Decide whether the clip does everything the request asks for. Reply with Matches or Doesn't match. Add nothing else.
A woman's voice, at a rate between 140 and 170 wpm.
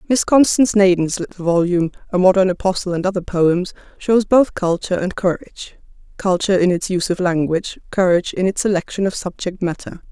Matches